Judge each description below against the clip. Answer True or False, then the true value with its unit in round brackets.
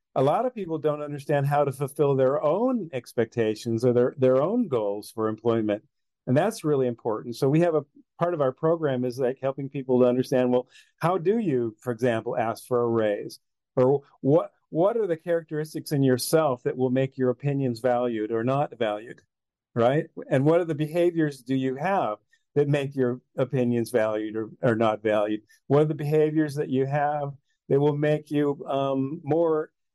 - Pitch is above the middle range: False (135 Hz)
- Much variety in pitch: False (3.8 semitones)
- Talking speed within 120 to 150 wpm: False (190 wpm)